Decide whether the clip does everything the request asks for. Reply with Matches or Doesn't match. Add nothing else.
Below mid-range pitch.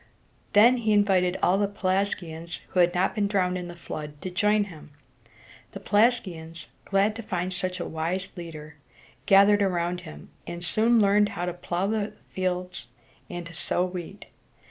Doesn't match